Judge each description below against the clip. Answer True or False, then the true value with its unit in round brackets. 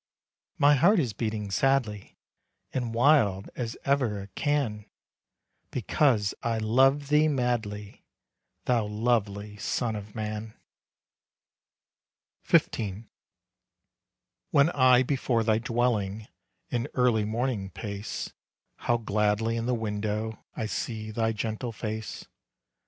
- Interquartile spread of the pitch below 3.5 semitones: True (3.0 semitones)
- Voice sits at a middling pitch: False (110 Hz)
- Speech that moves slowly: True (110 wpm)